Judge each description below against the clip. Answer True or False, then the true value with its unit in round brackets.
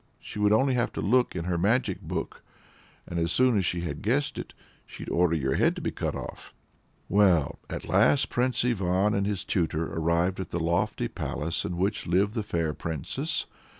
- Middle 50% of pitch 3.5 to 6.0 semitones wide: True (4.1 semitones)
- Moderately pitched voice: False (95 Hz)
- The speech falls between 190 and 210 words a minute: True (195 wpm)